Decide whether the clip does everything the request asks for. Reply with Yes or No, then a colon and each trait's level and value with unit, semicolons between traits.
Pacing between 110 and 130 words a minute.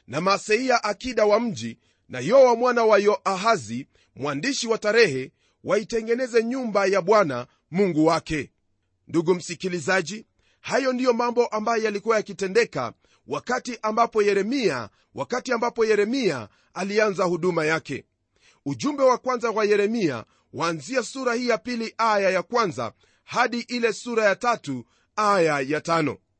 No: fast, 140 wpm